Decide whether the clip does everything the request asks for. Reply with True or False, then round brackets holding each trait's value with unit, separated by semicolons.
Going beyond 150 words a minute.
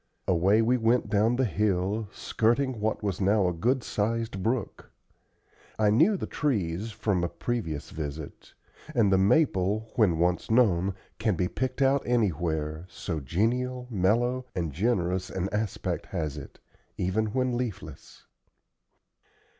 False (140 wpm)